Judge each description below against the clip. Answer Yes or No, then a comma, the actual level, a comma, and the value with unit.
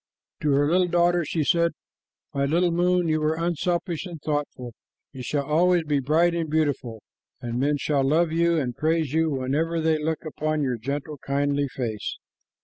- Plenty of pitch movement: No, average, 3.1 semitones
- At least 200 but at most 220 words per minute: No, average, 180 wpm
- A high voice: No, medium, 155 Hz